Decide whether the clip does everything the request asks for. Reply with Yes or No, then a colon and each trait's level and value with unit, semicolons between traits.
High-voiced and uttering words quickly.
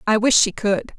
Yes: high, 215 Hz; fast, 245 wpm